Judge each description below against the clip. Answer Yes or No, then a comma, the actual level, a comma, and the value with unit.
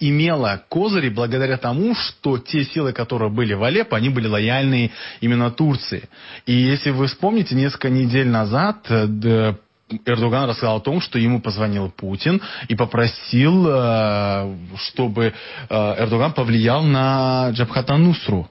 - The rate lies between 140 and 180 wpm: No, average, 125 wpm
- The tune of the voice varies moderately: Yes, average, 3.5 semitones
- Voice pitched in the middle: No, low, 120 Hz